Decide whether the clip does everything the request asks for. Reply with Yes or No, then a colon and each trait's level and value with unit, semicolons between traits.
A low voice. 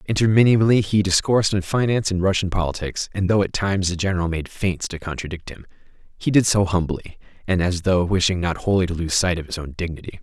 Yes: very low, 95 Hz